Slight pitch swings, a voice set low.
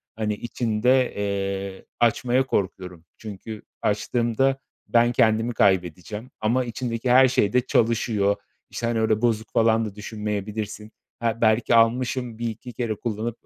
Yes: narrow, 2.3 semitones; low, 110 Hz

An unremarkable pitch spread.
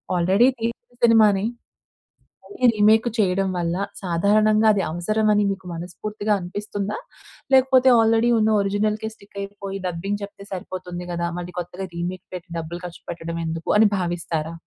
Yes: average, 3.4 semitones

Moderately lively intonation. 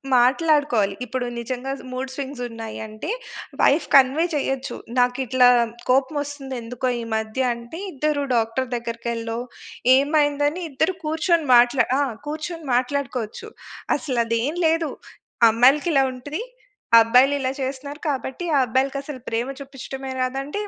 Yes: average, 3.0 semitones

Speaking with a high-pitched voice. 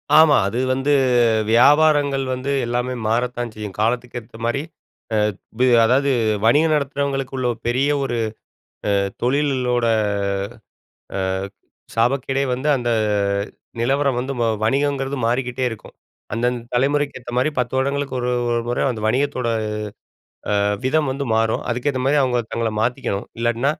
No: low, 130 Hz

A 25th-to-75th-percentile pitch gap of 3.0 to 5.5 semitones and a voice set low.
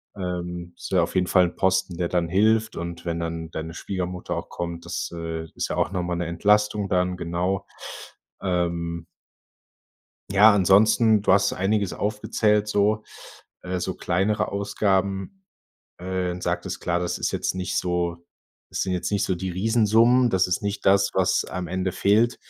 No: narrow, 2.6 semitones; very low, 95 Hz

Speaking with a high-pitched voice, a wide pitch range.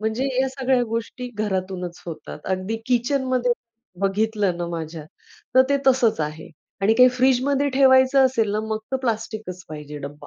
Yes: high, 220 Hz; wide, 5.9 semitones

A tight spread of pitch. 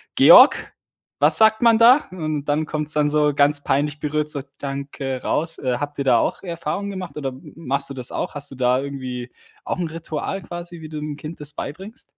No: average, 3.0 semitones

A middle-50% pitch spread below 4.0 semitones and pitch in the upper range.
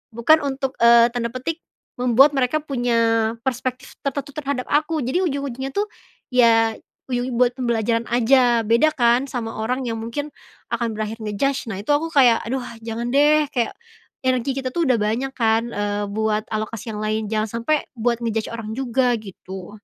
Yes: average, 3.1 semitones; high, 240 Hz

